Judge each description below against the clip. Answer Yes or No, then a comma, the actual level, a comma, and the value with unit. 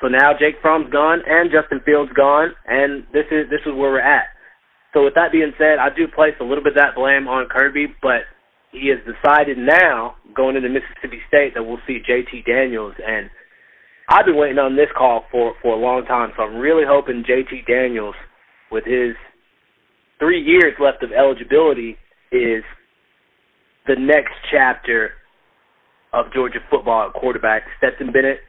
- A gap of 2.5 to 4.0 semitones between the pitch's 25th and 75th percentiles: Yes, average, 3.1 semitones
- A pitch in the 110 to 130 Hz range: No, medium, 140 Hz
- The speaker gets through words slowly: No, average, 175 wpm